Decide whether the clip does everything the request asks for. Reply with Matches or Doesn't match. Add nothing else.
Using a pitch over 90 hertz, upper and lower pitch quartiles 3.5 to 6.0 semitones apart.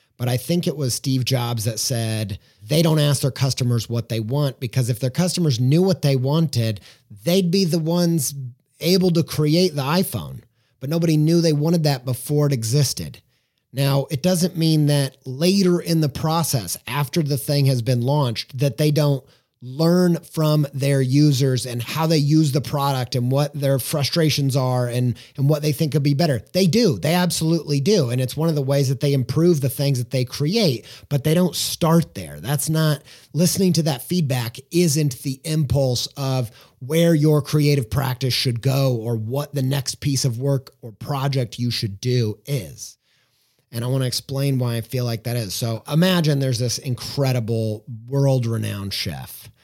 Matches